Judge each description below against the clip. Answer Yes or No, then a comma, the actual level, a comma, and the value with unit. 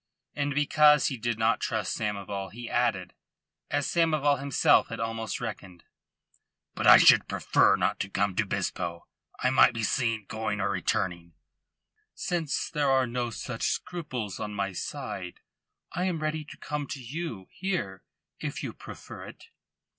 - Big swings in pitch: Yes, wide, 6.2 semitones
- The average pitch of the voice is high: No, low, 120 Hz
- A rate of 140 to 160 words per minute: Yes, average, 155 wpm